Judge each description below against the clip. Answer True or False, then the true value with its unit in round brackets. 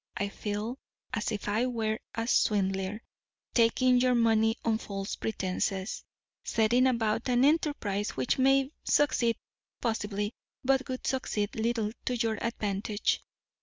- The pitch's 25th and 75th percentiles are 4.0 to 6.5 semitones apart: False (3.2 semitones)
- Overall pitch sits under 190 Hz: False (225 Hz)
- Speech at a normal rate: False (130 wpm)